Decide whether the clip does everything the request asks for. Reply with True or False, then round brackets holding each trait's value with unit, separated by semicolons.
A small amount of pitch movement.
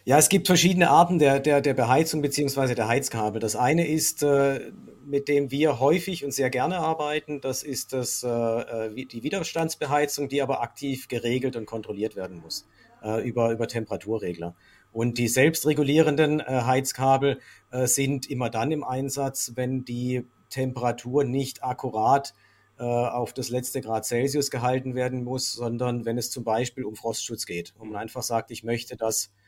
False (3.4 semitones)